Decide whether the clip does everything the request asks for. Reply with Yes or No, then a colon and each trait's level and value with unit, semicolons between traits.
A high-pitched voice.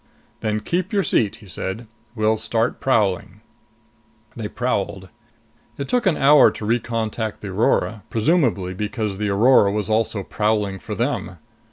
No: low, 110 Hz